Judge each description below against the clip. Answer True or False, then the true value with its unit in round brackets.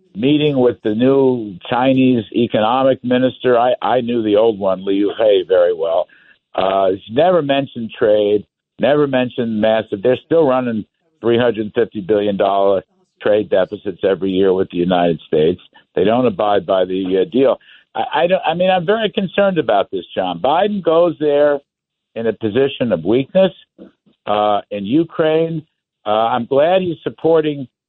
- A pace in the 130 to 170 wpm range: True (165 wpm)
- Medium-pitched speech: False (125 Hz)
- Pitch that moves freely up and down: True (7.4 semitones)